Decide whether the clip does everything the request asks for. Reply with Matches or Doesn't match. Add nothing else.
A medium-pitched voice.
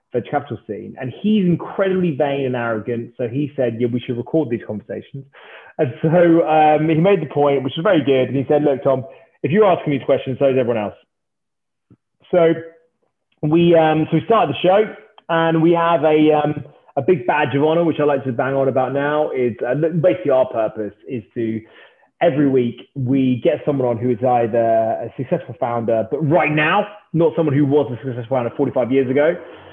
Matches